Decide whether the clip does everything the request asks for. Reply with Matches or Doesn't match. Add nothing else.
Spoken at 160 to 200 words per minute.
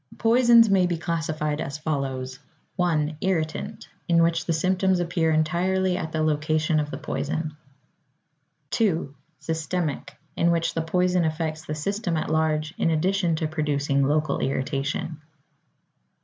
Doesn't match